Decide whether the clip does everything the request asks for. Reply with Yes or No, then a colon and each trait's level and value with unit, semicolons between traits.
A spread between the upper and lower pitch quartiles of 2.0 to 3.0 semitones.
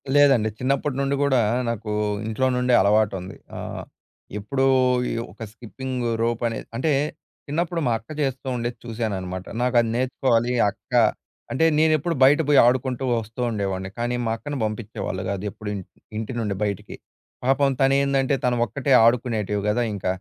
No: average, 3.8 semitones